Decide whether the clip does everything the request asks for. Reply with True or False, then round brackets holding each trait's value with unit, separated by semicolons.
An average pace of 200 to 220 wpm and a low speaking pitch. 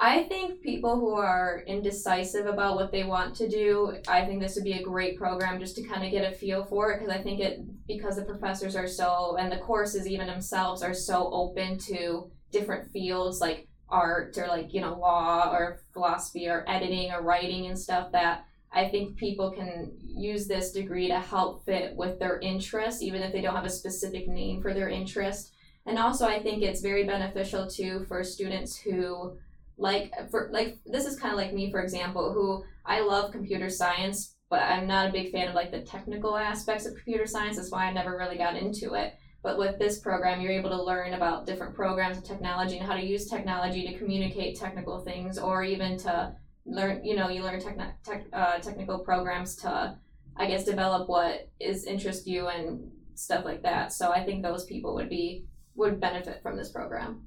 False (205 wpm; 190 Hz)